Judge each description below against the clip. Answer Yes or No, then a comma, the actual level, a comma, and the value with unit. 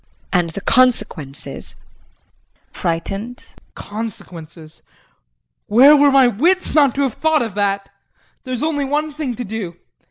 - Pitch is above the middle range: Yes, high, 230 Hz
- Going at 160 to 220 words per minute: No, slow, 135 wpm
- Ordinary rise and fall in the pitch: No, wide, 6.3 semitones